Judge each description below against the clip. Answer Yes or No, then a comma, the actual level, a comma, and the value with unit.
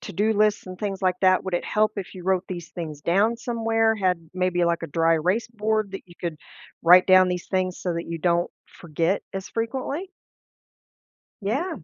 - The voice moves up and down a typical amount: Yes, average, 3.7 semitones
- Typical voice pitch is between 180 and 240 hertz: Yes, medium, 185 Hz